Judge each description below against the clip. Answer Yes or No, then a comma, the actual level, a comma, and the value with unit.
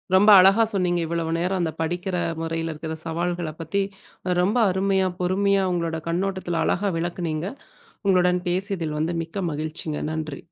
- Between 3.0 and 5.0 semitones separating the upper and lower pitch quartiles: No, narrow, 2.6 semitones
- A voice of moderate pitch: Yes, medium, 175 Hz